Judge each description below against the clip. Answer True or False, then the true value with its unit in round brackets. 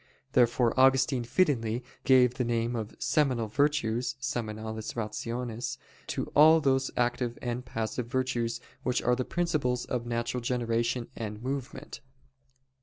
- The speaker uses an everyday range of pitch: False (2.2 semitones)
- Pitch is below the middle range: True (125 Hz)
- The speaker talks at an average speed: False (125 wpm)